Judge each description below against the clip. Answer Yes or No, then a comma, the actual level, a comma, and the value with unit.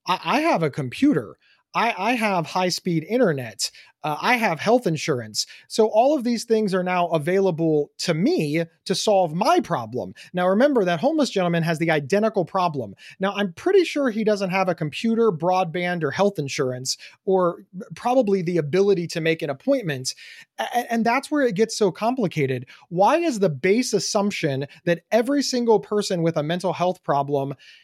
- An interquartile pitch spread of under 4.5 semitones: No, average, 5.2 semitones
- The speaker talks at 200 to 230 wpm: No, average, 175 wpm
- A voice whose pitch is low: No, high, 190 Hz